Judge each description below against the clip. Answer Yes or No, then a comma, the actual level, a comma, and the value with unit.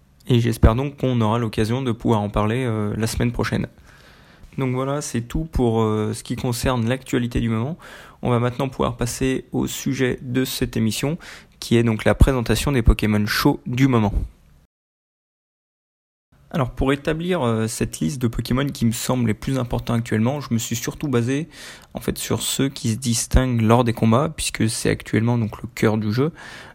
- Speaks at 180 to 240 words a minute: Yes, average, 190 wpm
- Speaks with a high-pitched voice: No, low, 120 Hz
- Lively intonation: No, average, 2.9 semitones